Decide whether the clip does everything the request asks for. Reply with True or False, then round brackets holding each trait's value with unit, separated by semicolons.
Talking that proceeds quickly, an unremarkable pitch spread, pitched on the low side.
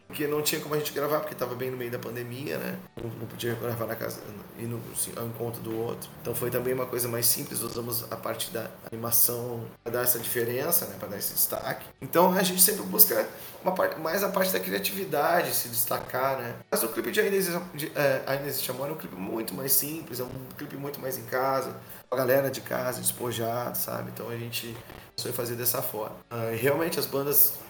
True (225 wpm; 3.6 semitones; 125 Hz)